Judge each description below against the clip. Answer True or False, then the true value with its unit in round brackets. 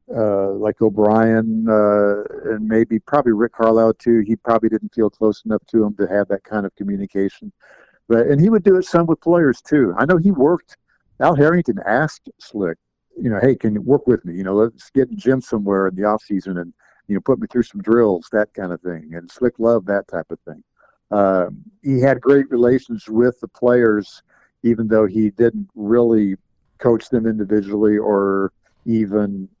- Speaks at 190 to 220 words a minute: True (200 wpm)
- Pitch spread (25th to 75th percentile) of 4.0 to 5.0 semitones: False (2.8 semitones)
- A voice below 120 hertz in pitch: True (110 Hz)